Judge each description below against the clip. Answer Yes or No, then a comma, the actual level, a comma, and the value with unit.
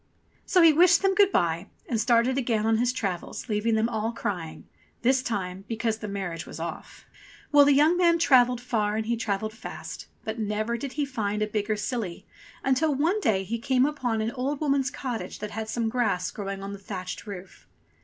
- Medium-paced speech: No, fast, 215 wpm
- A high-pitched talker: Yes, high, 225 Hz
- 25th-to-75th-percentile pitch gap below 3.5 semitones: No, average, 4.2 semitones